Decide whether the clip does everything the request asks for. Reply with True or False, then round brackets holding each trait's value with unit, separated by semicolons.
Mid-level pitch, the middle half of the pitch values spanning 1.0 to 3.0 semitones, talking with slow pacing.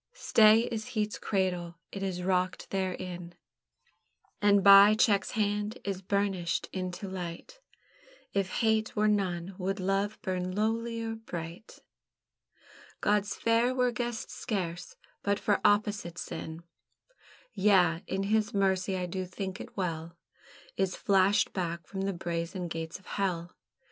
False (195 Hz; 2.6 semitones; 130 wpm)